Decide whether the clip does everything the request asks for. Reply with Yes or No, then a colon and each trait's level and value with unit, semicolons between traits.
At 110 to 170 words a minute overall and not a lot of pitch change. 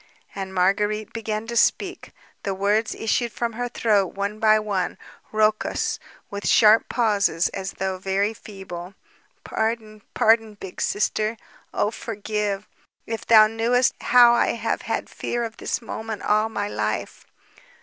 Yes: average, 140 wpm; narrow, 2.0 semitones